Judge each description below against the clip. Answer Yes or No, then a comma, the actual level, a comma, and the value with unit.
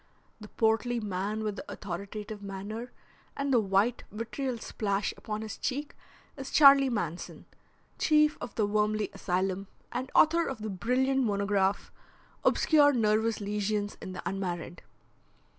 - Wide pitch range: No, average, 3.9 semitones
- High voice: Yes, high, 215 Hz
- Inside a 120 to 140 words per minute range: Yes, slow, 135 wpm